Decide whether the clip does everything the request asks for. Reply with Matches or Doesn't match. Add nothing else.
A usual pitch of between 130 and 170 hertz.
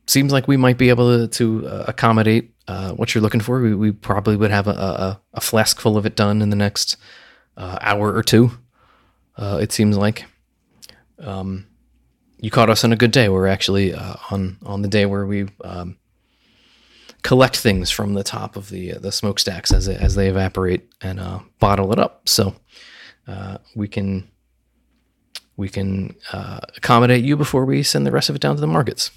Doesn't match